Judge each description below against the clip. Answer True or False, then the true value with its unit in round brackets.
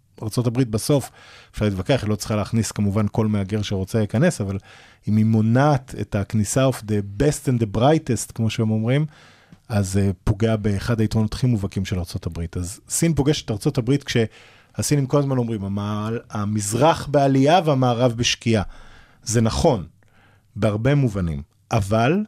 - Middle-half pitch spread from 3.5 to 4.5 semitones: True (4.0 semitones)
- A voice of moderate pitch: False (110 Hz)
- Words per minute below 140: False (150 wpm)